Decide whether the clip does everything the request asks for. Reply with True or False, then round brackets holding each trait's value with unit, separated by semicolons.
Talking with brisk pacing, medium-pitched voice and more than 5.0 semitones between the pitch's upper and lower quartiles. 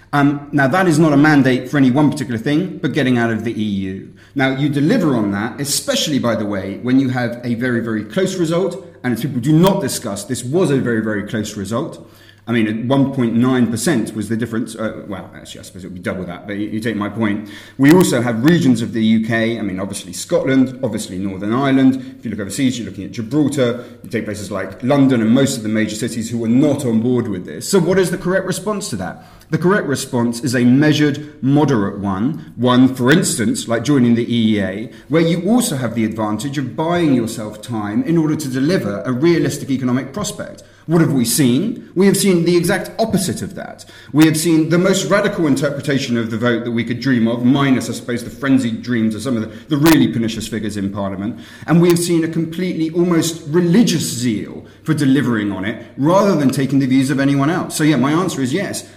False (225 wpm; 125 Hz; 5.4 semitones)